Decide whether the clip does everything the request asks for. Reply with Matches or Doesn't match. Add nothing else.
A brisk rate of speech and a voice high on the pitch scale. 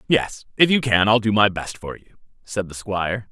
Doesn't match